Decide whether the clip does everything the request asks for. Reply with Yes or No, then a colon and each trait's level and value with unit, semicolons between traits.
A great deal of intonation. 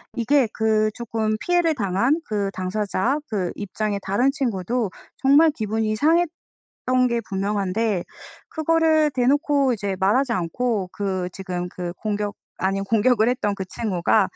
No: average, 4.6 semitones